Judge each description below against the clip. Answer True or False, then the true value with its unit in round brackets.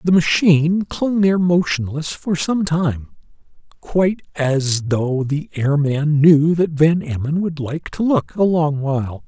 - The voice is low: False (155 Hz)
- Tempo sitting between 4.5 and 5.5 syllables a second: False (4.0 syllables/s)